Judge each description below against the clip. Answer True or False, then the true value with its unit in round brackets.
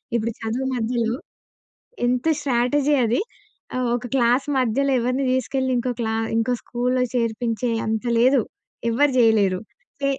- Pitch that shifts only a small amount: True (2.3 semitones)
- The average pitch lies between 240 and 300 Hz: True (245 Hz)